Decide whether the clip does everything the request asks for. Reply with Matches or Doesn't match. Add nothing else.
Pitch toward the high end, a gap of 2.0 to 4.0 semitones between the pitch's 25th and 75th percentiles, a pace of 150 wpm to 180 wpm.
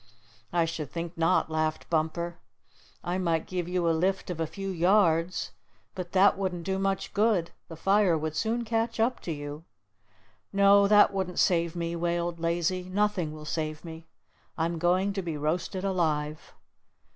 Doesn't match